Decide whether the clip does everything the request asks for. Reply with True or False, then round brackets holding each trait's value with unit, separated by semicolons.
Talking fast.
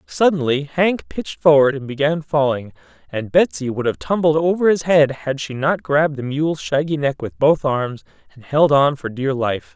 False (195 wpm)